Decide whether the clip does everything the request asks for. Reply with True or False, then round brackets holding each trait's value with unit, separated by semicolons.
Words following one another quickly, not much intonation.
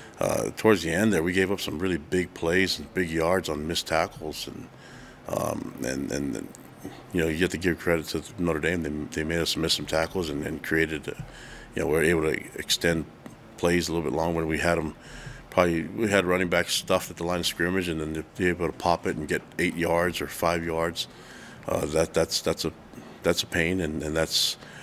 True (230 wpm; 2.0 semitones)